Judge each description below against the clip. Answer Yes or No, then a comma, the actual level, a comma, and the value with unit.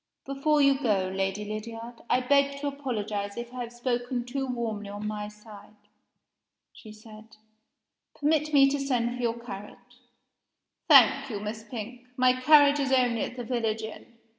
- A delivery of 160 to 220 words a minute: Yes, average, 165 wpm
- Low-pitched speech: No, high, 240 Hz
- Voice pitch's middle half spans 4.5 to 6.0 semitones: No, average, 3.9 semitones